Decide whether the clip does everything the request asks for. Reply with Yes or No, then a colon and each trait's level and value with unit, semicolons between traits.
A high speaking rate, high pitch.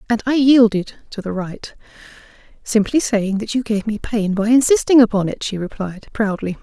No: average, 180 wpm; high, 220 Hz